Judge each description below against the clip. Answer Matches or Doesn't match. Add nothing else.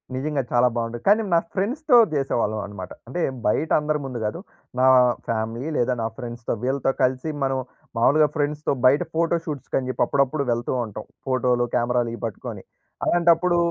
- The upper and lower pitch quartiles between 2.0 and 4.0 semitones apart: Doesn't match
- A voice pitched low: Matches